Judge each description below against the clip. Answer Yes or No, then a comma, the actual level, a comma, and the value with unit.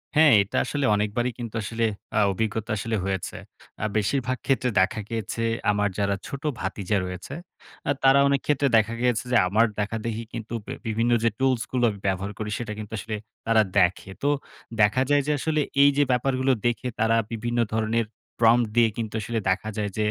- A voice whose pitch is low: Yes, low, 115 Hz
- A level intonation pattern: No, average, 3.2 semitones